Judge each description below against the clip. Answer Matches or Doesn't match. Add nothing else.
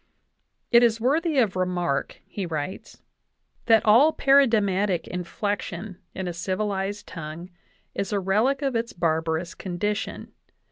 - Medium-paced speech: Doesn't match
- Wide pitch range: Doesn't match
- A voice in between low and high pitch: Doesn't match